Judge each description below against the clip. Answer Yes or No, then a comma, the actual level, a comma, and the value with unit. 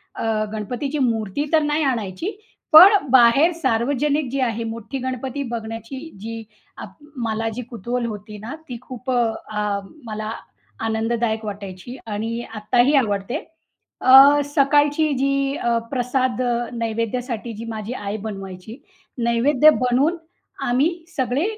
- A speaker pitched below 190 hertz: No, high, 240 Hz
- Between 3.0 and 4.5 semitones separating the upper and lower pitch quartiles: Yes, average, 3.6 semitones